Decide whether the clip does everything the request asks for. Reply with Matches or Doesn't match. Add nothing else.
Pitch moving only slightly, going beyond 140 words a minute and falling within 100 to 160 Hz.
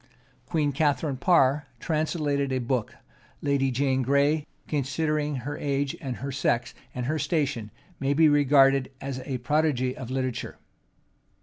Doesn't match